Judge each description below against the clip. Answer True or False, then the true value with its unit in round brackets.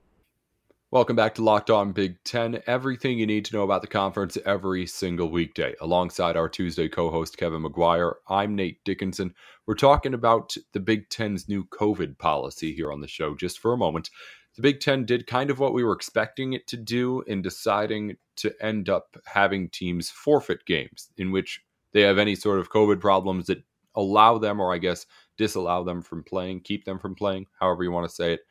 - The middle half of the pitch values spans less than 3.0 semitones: False (3.5 semitones)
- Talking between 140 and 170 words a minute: False (200 wpm)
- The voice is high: False (100 Hz)